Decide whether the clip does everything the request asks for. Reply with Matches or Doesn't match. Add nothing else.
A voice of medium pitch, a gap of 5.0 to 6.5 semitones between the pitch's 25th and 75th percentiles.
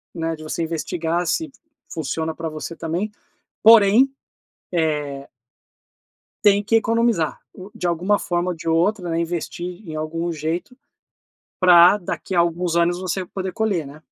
Doesn't match